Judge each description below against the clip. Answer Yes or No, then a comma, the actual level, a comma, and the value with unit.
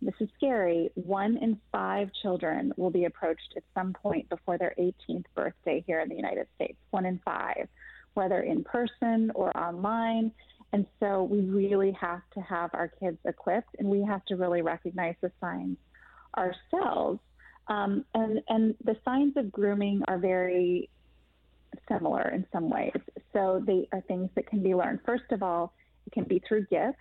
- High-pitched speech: Yes, high, 195 Hz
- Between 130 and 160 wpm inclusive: No, average, 175 wpm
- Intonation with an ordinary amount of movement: Yes, average, 3.7 semitones